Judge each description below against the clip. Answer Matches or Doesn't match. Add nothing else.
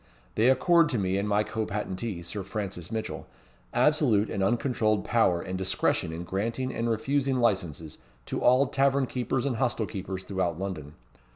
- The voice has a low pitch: Matches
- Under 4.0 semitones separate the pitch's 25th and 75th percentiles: Doesn't match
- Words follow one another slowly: Doesn't match